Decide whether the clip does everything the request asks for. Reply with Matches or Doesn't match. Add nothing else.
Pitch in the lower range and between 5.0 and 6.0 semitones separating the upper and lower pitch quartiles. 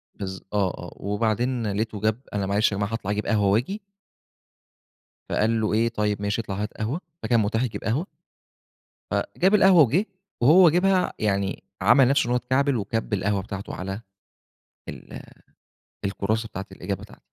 Doesn't match